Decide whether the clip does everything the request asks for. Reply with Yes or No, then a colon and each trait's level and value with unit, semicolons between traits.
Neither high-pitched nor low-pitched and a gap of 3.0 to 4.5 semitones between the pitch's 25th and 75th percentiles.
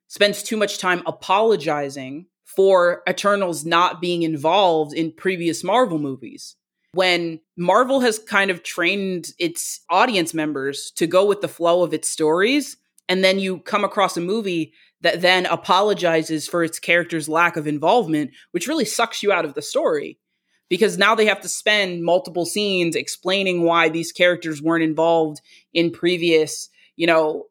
Yes: medium, 175 Hz; average, 3.4 semitones